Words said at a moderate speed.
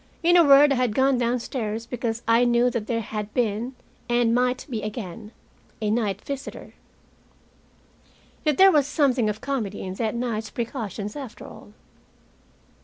Yes: average, 155 wpm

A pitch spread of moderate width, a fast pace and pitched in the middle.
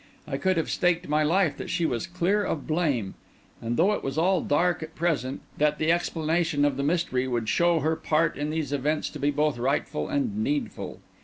Yes: average, 3.3 semitones; fast, 210 wpm; medium, 160 Hz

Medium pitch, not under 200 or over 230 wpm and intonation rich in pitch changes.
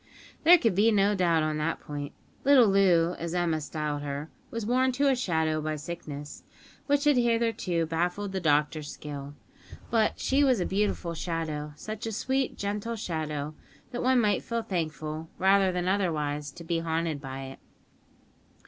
No: medium, 175 Hz; average, 165 wpm; wide, 5.9 semitones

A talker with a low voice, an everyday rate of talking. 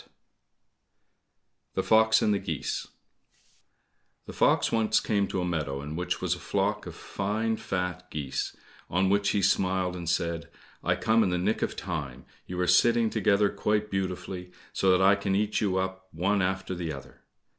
Yes: very low, 95 Hz; average, 175 wpm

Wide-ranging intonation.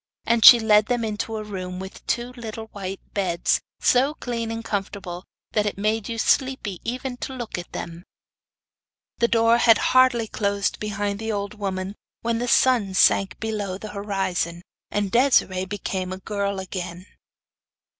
No: average, 3.2 semitones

